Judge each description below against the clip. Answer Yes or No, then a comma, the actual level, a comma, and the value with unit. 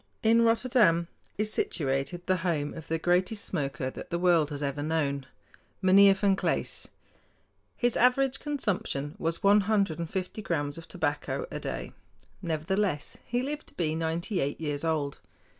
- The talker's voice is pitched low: No, medium, 170 Hz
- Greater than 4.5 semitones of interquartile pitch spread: Yes, average, 5.3 semitones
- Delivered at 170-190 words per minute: No, average, 160 wpm